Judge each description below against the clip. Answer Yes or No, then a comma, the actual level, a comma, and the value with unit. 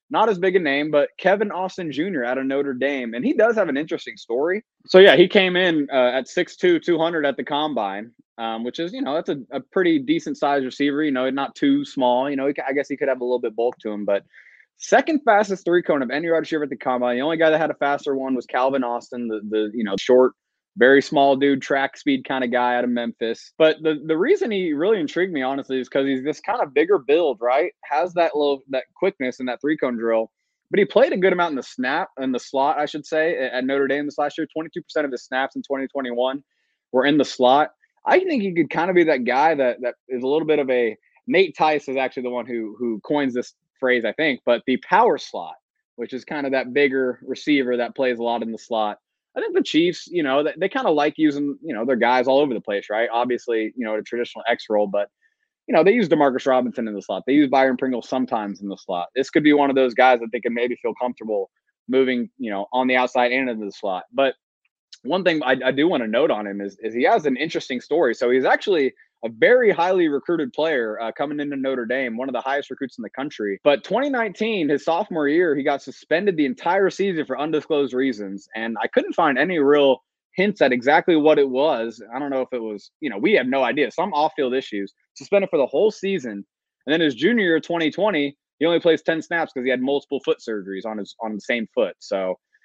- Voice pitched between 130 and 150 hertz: Yes, medium, 140 Hz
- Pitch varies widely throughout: No, average, 5.0 semitones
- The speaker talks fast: Yes, fast, 250 wpm